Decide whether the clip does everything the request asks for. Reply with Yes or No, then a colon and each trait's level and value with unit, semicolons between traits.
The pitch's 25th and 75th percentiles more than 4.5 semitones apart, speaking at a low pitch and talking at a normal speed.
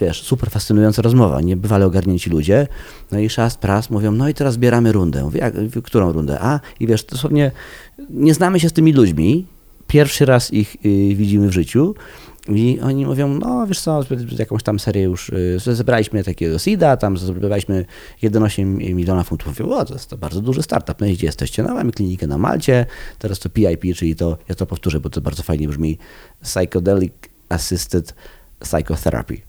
No: wide, 5.5 semitones; low, 105 Hz; fast, 175 wpm